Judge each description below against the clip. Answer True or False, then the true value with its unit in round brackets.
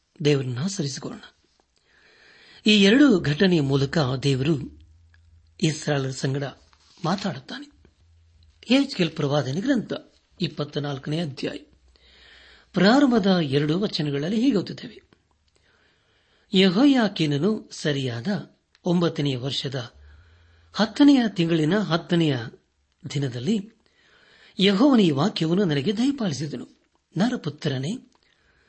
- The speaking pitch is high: False (155 Hz)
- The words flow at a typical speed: False (60 wpm)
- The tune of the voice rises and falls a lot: True (7.1 semitones)